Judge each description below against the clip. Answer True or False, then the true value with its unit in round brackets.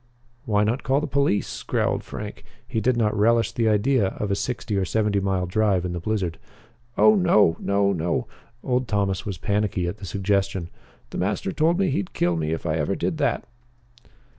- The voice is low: True (105 Hz)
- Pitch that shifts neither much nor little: True (3.7 semitones)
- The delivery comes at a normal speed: True (190 wpm)